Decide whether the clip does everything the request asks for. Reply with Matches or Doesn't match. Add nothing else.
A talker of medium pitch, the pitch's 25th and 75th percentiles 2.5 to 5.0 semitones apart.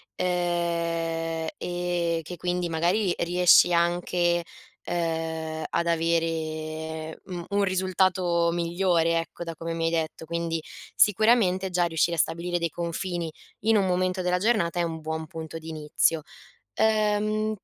Doesn't match